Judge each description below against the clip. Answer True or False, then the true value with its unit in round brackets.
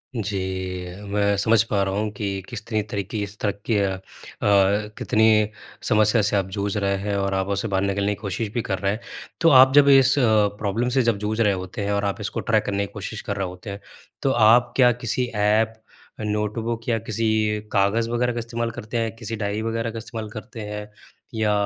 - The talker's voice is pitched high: False (105 Hz)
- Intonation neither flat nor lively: False (2.2 semitones)